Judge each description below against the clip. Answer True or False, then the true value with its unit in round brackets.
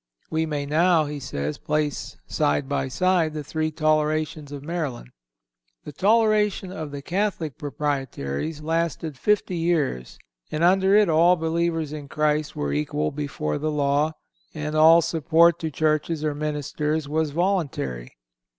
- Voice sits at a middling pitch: True (155 Hz)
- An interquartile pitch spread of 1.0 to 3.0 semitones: True (2.5 semitones)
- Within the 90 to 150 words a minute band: True (140 wpm)